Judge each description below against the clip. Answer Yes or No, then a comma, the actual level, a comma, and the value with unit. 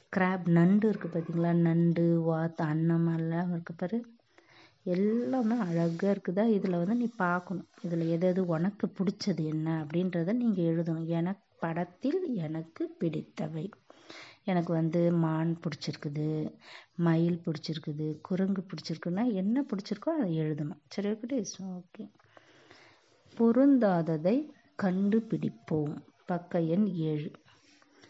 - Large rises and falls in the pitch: No, average, 3.5 semitones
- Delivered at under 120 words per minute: Yes, average, 100 wpm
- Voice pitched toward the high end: No, medium, 175 Hz